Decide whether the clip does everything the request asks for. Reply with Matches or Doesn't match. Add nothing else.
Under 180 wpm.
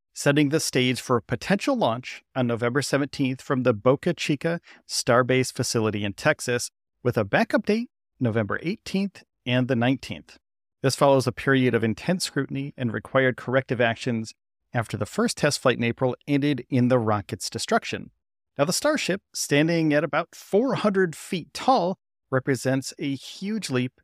Matches